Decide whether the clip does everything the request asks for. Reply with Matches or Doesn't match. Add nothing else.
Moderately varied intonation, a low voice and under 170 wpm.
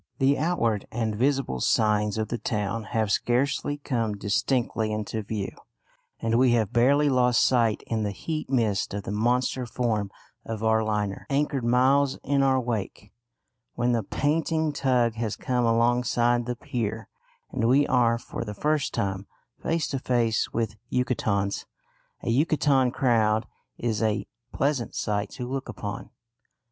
Matches